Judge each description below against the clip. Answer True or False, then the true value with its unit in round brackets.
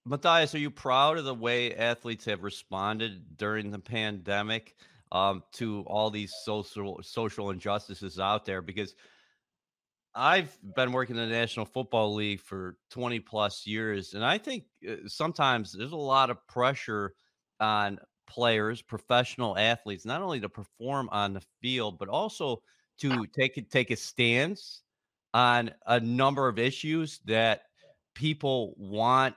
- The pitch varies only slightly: False (3.7 semitones)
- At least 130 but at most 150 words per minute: True (145 wpm)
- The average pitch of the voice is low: True (115 Hz)